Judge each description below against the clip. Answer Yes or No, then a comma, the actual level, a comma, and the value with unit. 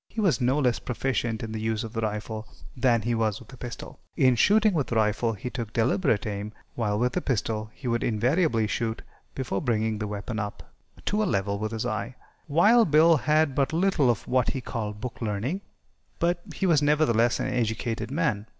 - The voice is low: Yes, low, 120 Hz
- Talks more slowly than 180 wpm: No, fast, 205 wpm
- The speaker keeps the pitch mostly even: No, average, 4.7 semitones